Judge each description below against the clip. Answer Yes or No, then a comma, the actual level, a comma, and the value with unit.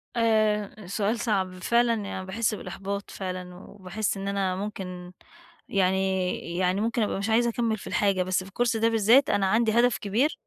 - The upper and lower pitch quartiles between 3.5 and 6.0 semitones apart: No, average, 3.1 semitones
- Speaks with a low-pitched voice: No, high, 200 Hz